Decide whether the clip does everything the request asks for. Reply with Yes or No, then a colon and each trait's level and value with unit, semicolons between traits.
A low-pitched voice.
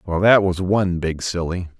Yes: very low, 90 Hz